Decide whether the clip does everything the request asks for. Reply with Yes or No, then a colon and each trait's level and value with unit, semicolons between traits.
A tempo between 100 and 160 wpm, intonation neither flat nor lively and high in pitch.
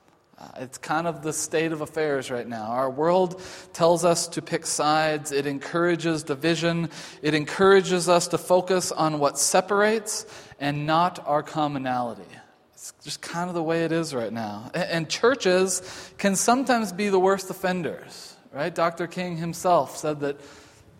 No: average, 155 wpm; average, 3.4 semitones; medium, 165 Hz